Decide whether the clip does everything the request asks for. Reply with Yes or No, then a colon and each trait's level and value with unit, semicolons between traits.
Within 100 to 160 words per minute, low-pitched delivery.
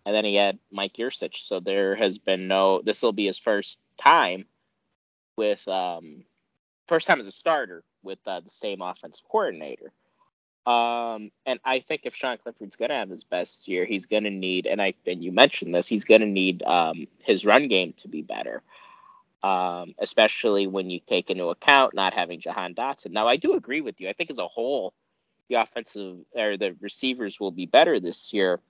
No: average, 195 wpm; low, 105 Hz